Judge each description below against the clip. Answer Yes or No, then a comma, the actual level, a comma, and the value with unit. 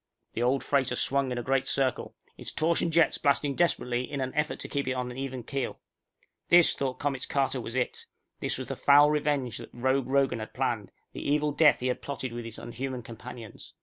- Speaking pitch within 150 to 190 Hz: No, low, 135 Hz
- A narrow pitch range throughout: Yes, narrow, 2.2 semitones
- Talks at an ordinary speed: No, fast, 210 wpm